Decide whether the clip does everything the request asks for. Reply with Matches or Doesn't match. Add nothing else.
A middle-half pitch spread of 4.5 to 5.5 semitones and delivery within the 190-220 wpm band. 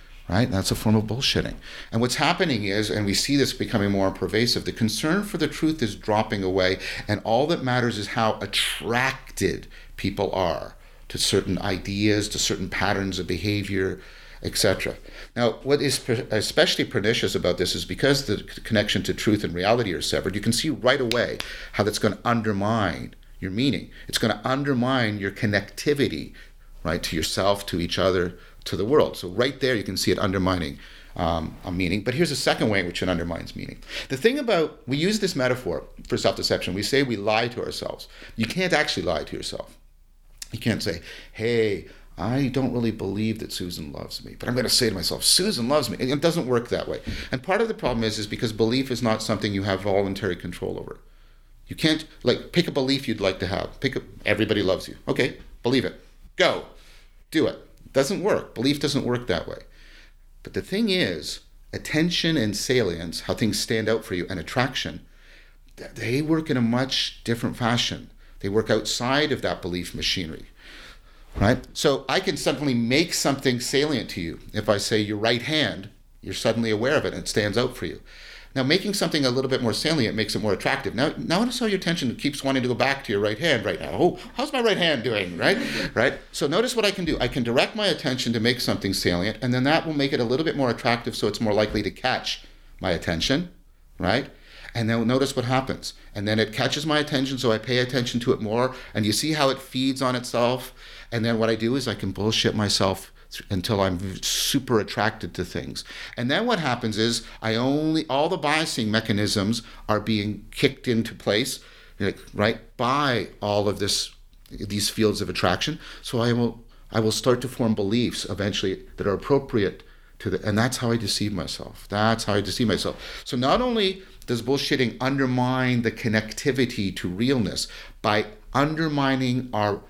Matches